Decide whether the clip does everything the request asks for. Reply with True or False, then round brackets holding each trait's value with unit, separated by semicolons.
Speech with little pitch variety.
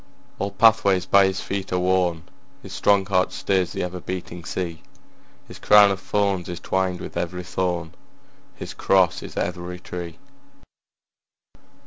True (1.9 semitones)